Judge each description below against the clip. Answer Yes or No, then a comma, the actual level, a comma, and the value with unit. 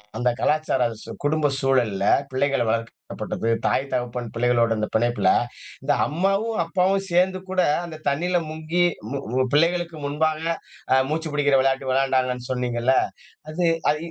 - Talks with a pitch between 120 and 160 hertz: Yes, medium, 140 Hz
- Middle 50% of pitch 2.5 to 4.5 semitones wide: No, average, 5.0 semitones